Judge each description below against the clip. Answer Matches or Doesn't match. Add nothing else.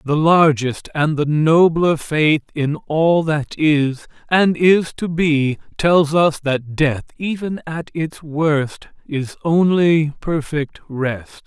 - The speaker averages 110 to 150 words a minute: Matches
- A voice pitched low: Doesn't match